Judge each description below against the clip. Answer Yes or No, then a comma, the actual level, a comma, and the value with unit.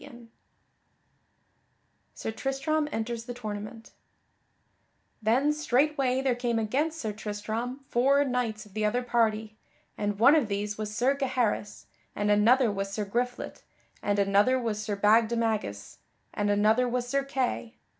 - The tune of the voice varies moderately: Yes, average, 3.3 semitones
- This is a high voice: Yes, high, 230 Hz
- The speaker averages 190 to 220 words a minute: No, slow, 135 wpm